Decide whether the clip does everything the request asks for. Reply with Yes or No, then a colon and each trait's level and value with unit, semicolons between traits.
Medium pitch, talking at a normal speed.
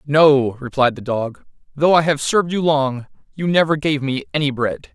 Yes: medium, 145 Hz; average, 195 wpm